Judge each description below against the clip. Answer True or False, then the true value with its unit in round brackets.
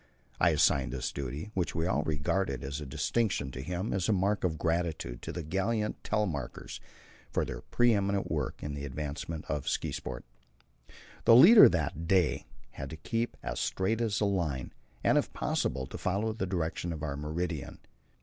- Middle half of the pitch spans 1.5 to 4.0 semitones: False (5.3 semitones)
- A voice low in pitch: True (85 Hz)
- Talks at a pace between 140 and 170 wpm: False (180 wpm)